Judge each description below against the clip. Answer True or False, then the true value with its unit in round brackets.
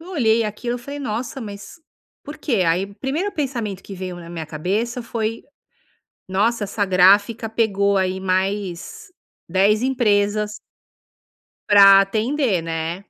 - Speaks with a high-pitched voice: True (210 Hz)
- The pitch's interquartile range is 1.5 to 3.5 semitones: False (3.9 semitones)